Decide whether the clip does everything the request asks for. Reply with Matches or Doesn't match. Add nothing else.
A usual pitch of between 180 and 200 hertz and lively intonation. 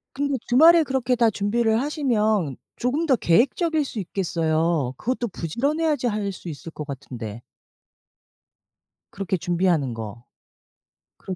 Doesn't match